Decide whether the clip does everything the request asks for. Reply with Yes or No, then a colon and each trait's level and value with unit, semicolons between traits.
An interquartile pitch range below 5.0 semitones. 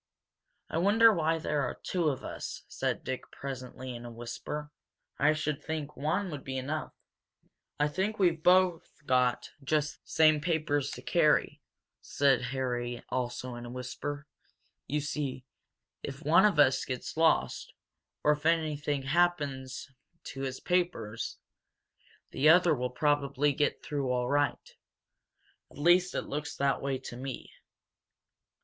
Yes: average, 3.3 semitones